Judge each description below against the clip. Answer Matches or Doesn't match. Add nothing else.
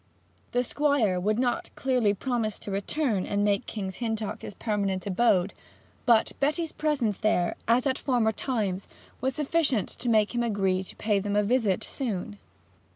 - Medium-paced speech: Matches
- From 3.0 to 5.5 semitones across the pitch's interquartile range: Matches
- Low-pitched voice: Doesn't match